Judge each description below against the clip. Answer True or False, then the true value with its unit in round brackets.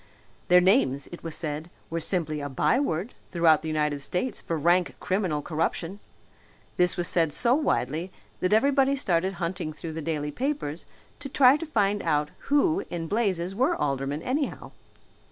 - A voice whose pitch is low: False (175 Hz)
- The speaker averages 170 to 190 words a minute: False (160 wpm)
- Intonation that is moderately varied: False (6.2 semitones)